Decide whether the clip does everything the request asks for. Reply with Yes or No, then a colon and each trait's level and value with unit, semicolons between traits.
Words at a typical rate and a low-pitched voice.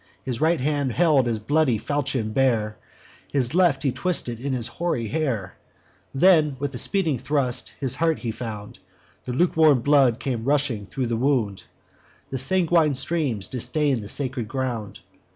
Yes: average, 155 wpm; low, 130 Hz